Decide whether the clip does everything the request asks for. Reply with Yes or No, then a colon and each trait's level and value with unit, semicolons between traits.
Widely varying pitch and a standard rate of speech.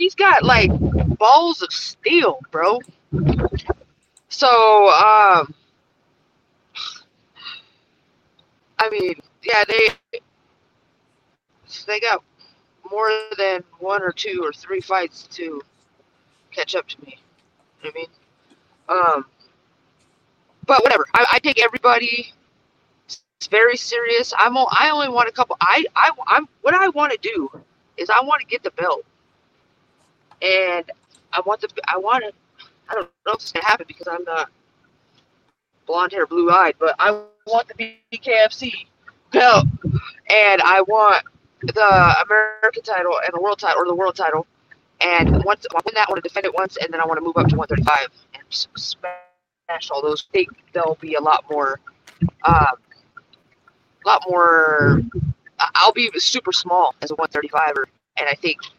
Yes: wide, 7.4 semitones; average, 155 wpm